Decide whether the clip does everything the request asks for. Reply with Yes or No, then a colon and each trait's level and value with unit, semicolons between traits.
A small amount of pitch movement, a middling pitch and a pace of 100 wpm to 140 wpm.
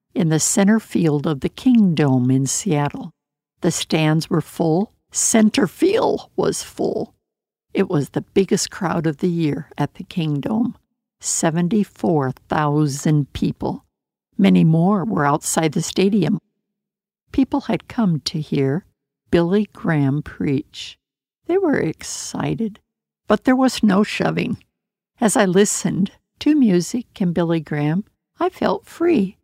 No: wide, 5.4 semitones; medium, 180 Hz; slow, 135 wpm